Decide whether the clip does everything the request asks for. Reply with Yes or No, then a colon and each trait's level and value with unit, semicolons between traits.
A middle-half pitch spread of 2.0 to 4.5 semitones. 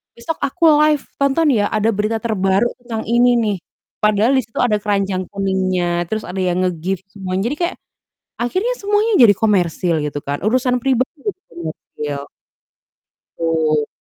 No: average, 5.1 semitones